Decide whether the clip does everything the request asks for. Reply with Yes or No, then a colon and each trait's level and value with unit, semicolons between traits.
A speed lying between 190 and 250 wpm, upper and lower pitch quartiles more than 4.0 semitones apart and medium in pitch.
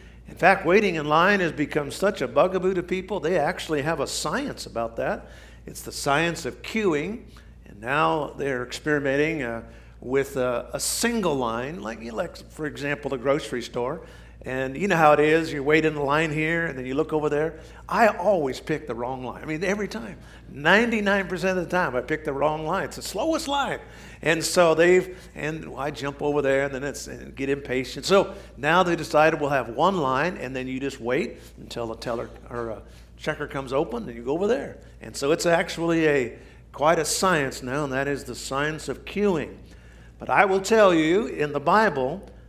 Yes: average, 200 wpm; average, 4.7 semitones; medium, 150 Hz